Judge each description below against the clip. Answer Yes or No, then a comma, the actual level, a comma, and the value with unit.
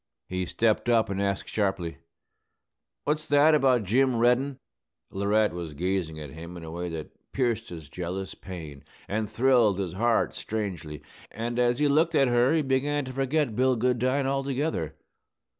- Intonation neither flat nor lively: No, wide, 6.3 semitones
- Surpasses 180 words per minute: No, average, 160 wpm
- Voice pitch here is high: No, low, 115 Hz